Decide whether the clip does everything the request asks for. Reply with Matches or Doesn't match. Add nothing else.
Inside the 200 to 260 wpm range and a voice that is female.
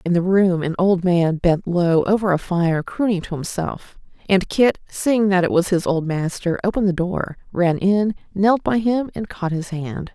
Matches